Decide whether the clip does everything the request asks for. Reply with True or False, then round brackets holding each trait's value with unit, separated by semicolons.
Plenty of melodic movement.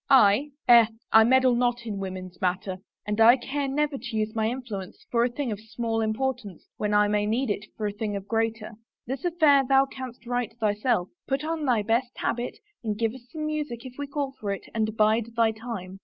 False (3.7 semitones)